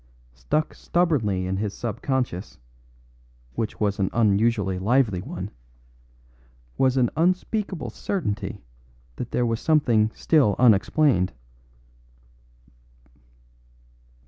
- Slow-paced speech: Yes, slow, 90 wpm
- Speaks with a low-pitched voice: Yes, low, 115 Hz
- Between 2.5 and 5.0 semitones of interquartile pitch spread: No, wide, 5.6 semitones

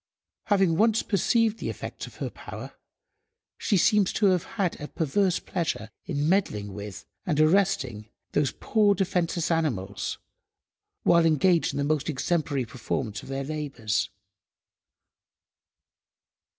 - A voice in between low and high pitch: Yes, medium, 160 Hz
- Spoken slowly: Yes, slow, 125 wpm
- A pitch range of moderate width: No, wide, 6.2 semitones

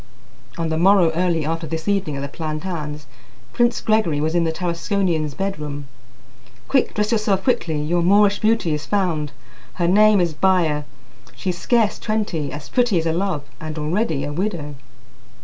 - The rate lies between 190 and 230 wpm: No, average, 165 wpm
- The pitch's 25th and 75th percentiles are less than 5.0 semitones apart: Yes, average, 4.6 semitones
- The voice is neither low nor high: Yes, medium, 170 Hz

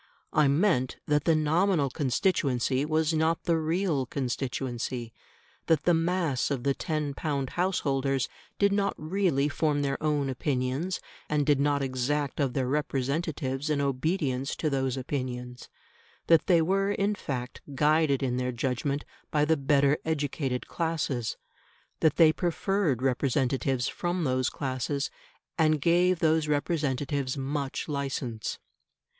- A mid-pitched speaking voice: Yes, medium, 145 Hz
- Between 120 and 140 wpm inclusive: Yes, slow, 135 wpm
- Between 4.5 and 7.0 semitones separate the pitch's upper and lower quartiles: No, average, 3.3 semitones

